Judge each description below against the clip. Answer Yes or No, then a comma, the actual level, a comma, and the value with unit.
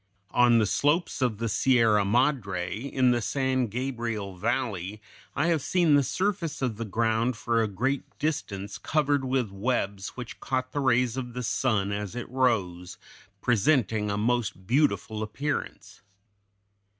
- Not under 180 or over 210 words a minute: No, average, 150 wpm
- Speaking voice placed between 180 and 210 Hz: No, low, 120 Hz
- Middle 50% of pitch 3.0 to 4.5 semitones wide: Yes, average, 4.0 semitones